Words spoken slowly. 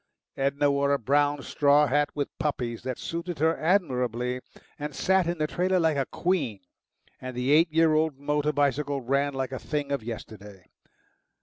No: average, 175 wpm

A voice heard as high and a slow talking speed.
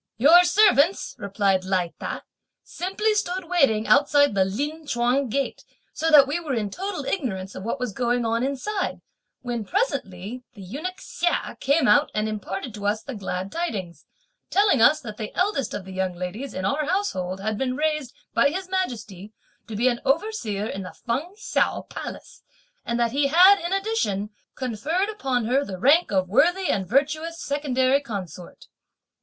No: very high, 255 Hz; average, 170 wpm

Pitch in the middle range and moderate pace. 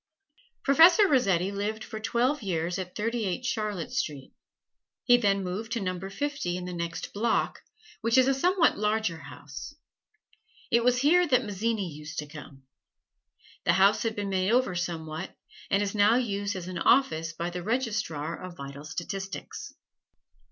No: high, 200 Hz; average, 160 wpm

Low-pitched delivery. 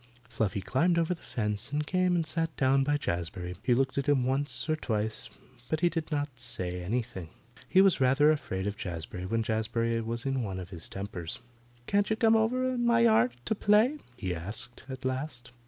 Yes: low, 130 Hz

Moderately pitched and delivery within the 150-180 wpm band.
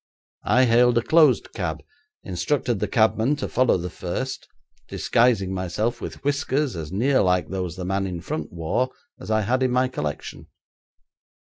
No: low, 110 Hz; average, 165 wpm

